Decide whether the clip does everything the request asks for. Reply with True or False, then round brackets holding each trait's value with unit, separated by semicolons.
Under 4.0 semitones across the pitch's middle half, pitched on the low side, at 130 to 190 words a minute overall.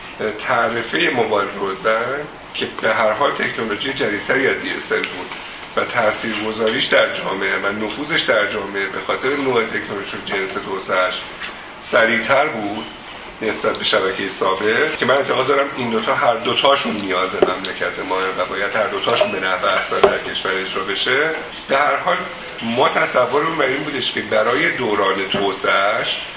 True (2.8 semitones; 100 Hz; 150 wpm)